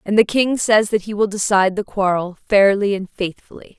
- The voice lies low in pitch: No, high, 200 Hz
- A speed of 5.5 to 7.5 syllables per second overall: No, 5.2 syllables/s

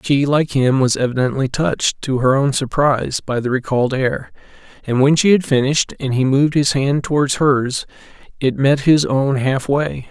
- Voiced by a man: Yes, male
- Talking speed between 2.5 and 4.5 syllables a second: No, 4.9 syllables/s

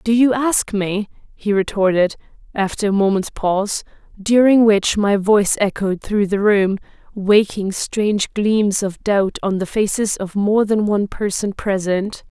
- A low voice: No, high, 205 Hz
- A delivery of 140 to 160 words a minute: Yes, average, 155 wpm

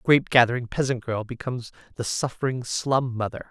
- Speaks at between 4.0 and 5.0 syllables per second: No, 6.1 syllables/s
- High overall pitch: No, low, 125 Hz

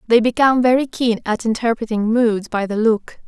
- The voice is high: Yes, high, 230 Hz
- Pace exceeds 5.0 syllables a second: Yes, 5.4 syllables/s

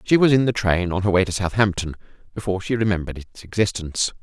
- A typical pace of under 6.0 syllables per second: No, 6.8 syllables/s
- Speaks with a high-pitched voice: No, low, 100 Hz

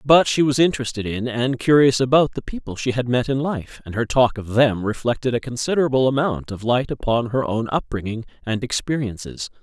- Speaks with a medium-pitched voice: No, low, 125 Hz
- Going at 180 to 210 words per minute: Yes, average, 200 wpm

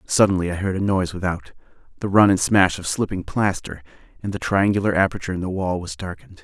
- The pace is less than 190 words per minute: No, fast, 205 wpm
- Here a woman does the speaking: No, male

